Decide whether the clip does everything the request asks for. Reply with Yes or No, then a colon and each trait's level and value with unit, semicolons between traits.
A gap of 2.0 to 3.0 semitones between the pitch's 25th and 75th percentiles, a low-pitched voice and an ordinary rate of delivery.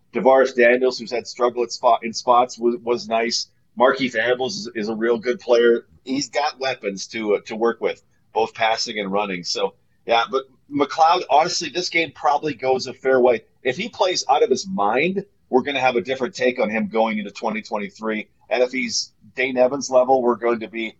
Yes: narrow, 2.5 semitones; low, 120 Hz; average, 195 wpm